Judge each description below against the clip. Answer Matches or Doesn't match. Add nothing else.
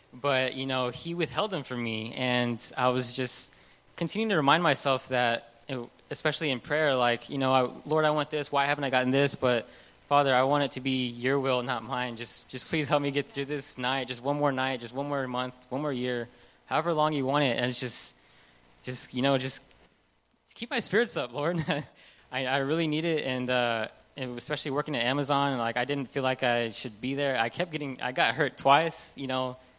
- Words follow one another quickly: Matches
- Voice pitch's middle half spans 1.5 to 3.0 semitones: Matches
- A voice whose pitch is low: Matches